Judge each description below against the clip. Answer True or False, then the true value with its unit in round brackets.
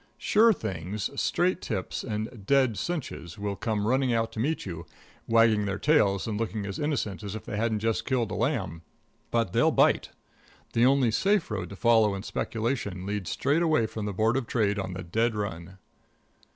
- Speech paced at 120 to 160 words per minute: False (190 wpm)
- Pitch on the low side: True (110 Hz)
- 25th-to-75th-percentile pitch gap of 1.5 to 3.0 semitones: False (3.6 semitones)